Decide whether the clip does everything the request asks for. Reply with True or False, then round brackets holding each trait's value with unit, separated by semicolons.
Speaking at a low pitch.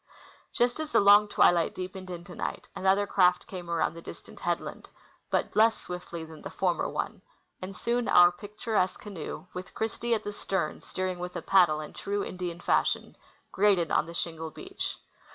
False (185 Hz)